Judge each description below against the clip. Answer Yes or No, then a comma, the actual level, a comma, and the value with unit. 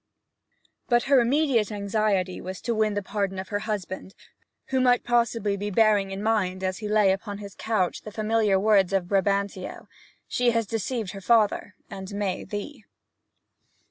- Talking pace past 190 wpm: No, average, 165 wpm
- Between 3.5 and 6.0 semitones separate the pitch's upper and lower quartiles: No, narrow, 2.6 semitones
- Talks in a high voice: Yes, high, 205 Hz